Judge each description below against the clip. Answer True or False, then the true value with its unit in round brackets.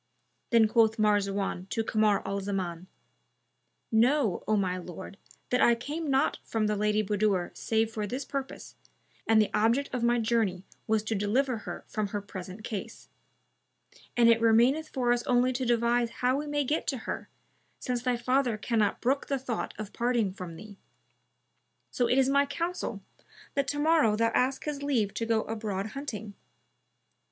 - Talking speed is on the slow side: False (170 wpm)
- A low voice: False (230 Hz)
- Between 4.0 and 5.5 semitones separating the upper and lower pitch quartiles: False (3.5 semitones)